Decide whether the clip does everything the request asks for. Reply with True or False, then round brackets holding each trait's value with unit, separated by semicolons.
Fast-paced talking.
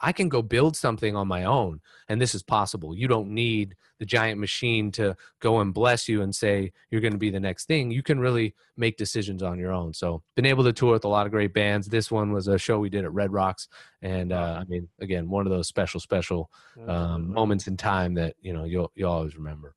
True (250 wpm)